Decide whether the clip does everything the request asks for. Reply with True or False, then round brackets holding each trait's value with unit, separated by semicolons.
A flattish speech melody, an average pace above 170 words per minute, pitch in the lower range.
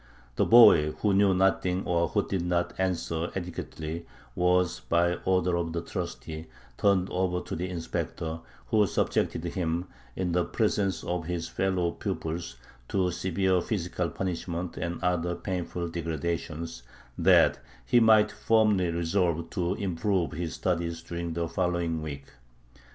False (1.9 semitones; 140 wpm; 85 Hz)